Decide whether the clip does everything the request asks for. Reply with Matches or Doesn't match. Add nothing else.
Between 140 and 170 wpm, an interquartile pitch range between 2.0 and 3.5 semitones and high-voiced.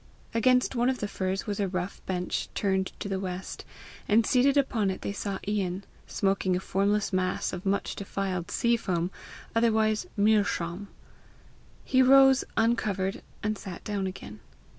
Matches